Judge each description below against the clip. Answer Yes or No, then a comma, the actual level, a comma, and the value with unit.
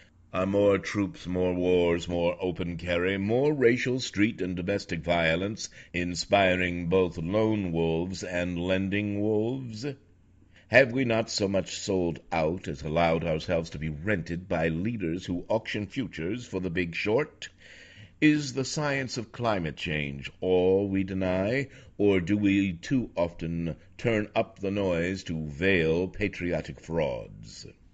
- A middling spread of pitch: Yes, average, 3.3 semitones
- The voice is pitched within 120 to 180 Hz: No, very low, 95 Hz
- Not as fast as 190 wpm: Yes, average, 140 wpm